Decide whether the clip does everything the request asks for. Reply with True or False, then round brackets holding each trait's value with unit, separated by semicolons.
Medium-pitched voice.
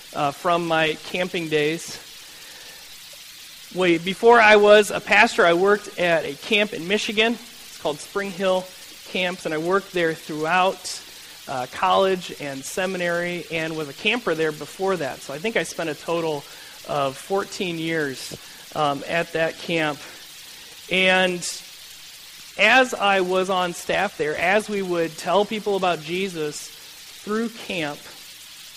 True (180 Hz)